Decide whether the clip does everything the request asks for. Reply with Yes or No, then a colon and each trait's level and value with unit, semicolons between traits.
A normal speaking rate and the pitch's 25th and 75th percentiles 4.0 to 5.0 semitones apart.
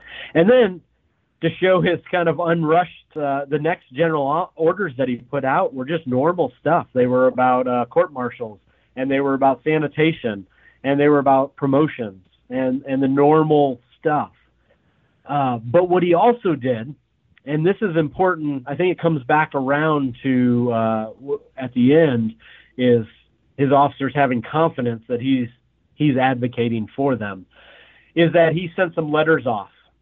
Yes: average, 165 wpm; average, 4.5 semitones